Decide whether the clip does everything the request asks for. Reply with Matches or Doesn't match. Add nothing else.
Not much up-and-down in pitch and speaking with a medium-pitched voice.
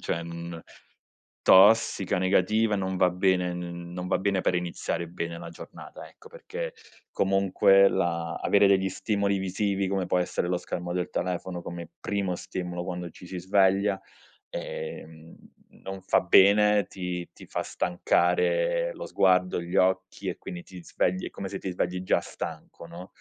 Doesn't match